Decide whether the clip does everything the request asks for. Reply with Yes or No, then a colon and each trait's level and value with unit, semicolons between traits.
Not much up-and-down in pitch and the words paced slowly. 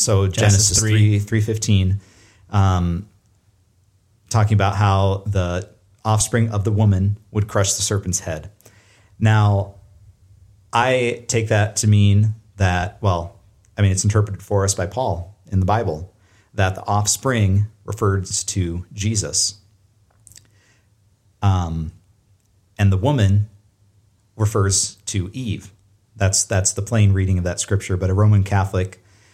Yes: narrow, 1.5 semitones; slow, 130 wpm